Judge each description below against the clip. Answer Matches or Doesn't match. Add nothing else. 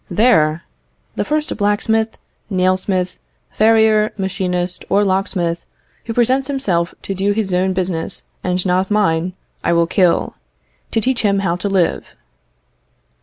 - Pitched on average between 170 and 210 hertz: Matches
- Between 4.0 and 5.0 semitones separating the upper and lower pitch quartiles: Doesn't match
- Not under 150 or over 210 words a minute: Doesn't match